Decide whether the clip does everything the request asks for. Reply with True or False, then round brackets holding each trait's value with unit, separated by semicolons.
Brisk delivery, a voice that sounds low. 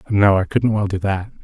True (250 wpm; 100 Hz)